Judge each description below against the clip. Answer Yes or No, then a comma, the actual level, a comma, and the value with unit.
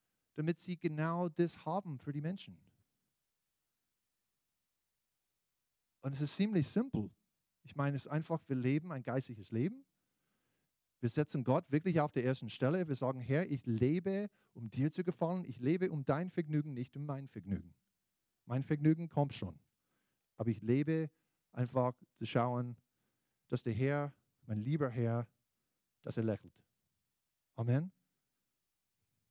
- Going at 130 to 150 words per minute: Yes, average, 140 wpm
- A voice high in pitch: No, medium, 140 Hz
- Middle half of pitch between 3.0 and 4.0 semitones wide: No, average, 4.5 semitones